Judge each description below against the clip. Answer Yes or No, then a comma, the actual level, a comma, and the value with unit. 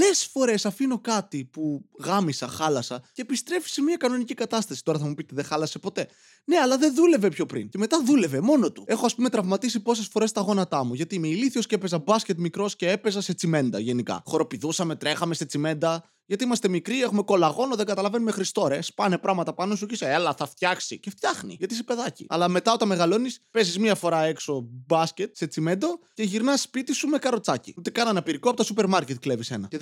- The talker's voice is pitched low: No, high, 200 Hz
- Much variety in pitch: Yes, wide, 6.6 semitones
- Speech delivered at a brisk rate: Yes, fast, 205 wpm